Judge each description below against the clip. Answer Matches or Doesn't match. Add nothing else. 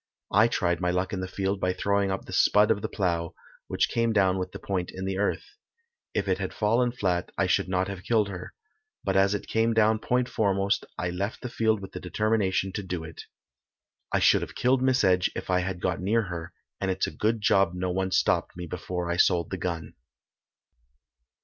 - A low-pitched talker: Matches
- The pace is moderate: Doesn't match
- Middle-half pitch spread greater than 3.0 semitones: Doesn't match